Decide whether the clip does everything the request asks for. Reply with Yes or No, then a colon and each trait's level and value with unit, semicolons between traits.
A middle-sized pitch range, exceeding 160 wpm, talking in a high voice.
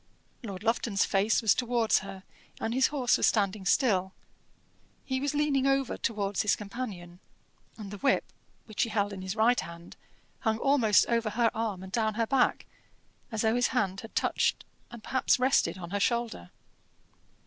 Yes: average, 3.7 semitones; average, 170 wpm; high, 220 Hz